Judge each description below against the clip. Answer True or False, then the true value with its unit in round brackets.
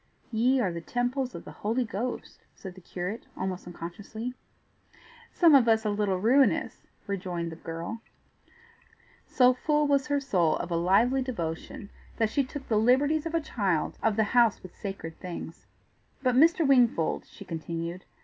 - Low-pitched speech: False (220 Hz)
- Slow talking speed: False (165 wpm)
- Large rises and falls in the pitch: True (6.2 semitones)